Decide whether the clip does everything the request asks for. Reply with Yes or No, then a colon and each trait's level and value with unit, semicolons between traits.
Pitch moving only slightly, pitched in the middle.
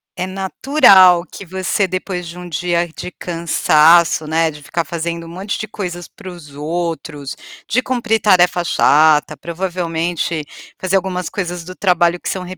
Yes: narrow, 2.0 semitones; medium, 175 Hz